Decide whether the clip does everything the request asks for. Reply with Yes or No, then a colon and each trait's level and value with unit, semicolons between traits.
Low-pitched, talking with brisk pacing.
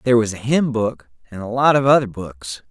Yes: low, 115 Hz; fast, 245 wpm